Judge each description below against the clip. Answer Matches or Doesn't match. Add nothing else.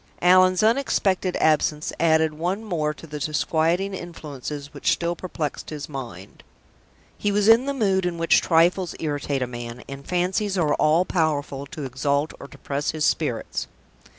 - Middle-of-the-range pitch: Matches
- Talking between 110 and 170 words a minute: Matches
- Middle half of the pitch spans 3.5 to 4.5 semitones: Matches